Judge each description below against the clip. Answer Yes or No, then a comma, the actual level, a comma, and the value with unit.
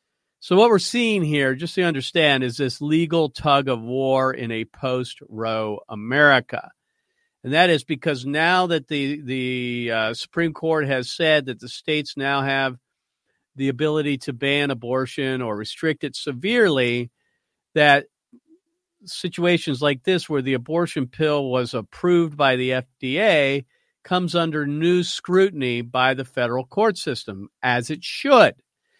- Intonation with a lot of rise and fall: No, average, 4.7 semitones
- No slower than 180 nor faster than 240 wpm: No, average, 145 wpm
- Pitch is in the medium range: Yes, medium, 145 Hz